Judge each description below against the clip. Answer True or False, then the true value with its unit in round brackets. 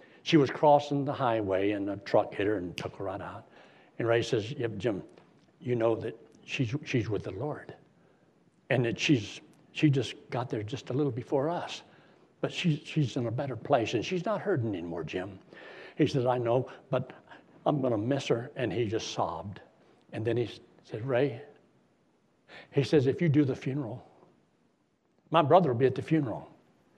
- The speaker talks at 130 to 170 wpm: False (185 wpm)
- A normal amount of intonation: True (4.2 semitones)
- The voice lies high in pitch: False (135 Hz)